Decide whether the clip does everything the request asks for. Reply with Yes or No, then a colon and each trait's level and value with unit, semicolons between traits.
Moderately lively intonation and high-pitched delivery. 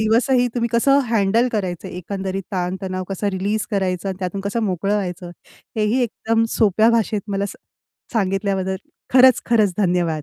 Yes: average, 3.1 semitones; high, 200 Hz